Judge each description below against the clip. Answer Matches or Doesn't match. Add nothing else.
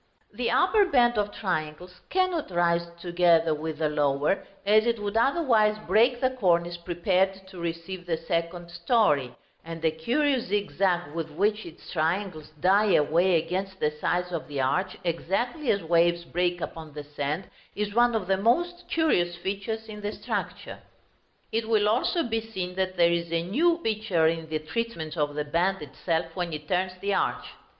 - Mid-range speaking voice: Matches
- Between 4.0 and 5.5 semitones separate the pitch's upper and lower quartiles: Matches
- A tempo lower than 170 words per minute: Doesn't match